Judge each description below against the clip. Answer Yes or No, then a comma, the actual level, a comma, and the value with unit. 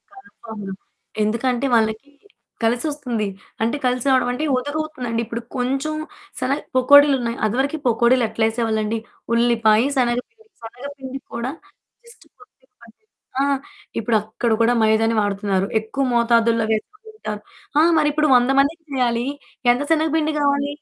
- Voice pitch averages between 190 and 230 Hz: No, high, 245 Hz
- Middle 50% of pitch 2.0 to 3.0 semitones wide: No, average, 3.8 semitones